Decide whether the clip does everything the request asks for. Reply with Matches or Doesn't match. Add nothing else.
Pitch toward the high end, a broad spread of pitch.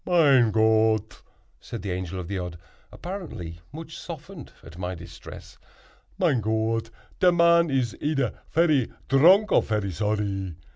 Doesn't match